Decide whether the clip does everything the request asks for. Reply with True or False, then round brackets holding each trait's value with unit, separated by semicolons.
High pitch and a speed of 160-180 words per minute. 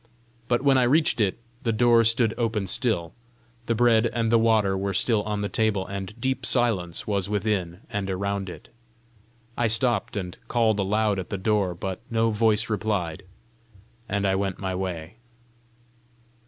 False (105 Hz; 165 wpm)